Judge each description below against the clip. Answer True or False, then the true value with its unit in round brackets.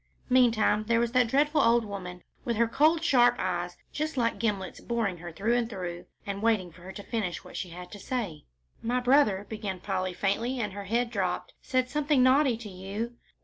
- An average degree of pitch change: True (4.5 semitones)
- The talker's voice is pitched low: False (225 Hz)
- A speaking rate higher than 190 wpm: True (200 wpm)